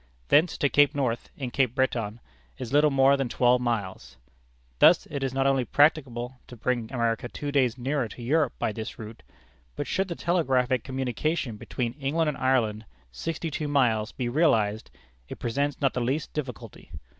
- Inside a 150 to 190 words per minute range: Yes, average, 175 wpm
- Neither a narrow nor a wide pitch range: Yes, average, 3.3 semitones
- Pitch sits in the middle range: No, low, 130 Hz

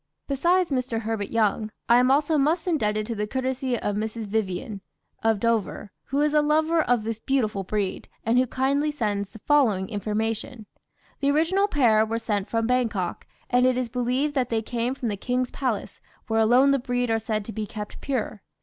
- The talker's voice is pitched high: Yes, high, 235 Hz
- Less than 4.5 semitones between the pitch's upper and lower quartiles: Yes, average, 3.9 semitones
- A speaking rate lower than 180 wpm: No, average, 195 wpm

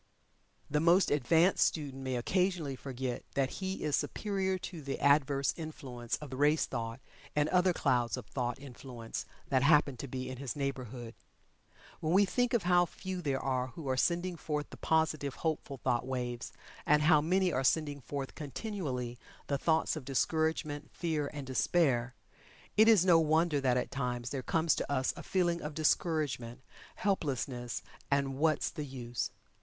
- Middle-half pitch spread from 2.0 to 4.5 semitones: Yes, average, 4.1 semitones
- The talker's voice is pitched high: No, medium, 145 Hz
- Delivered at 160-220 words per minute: Yes, average, 170 wpm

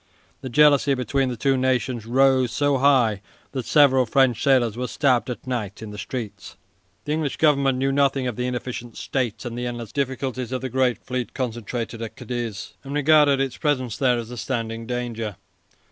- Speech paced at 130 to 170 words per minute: No, average, 185 wpm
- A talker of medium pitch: No, low, 125 Hz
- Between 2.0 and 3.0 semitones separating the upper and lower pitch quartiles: Yes, narrow, 2.4 semitones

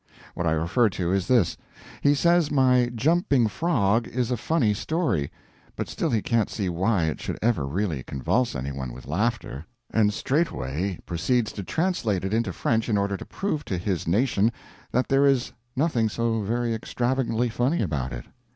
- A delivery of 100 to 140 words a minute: No, average, 180 wpm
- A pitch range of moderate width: No, wide, 5.7 semitones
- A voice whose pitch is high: No, low, 110 Hz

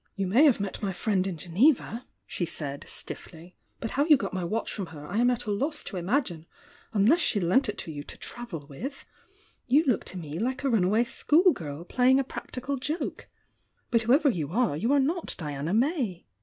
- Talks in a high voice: Yes, high, 220 Hz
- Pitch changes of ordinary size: No, wide, 7.0 semitones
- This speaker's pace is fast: Yes, fast, 210 wpm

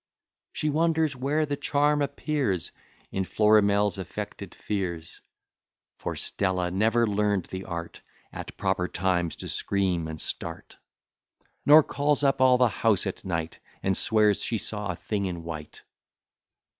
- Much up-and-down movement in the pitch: Yes, wide, 6.2 semitones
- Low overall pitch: Yes, low, 100 Hz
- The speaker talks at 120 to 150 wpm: Yes, average, 140 wpm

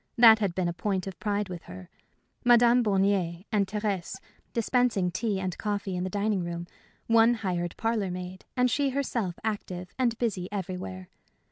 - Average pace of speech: Yes, average, 165 wpm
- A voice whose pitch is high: Yes, high, 200 Hz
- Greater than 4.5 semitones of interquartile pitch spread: No, average, 3.8 semitones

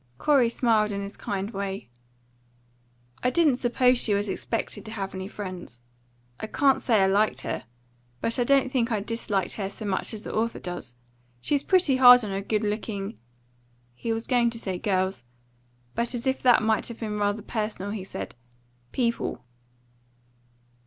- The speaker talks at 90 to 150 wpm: No, average, 175 wpm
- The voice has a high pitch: Yes, high, 215 Hz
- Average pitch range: Yes, average, 3.4 semitones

